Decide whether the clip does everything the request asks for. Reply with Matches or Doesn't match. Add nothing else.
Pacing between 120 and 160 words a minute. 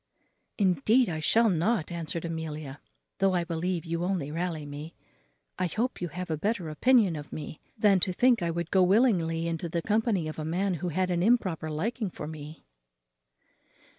Doesn't match